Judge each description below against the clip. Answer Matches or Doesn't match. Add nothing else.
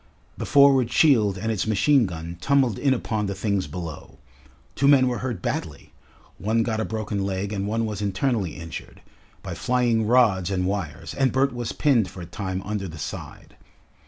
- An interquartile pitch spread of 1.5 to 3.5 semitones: Doesn't match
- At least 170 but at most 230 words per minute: Matches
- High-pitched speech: Doesn't match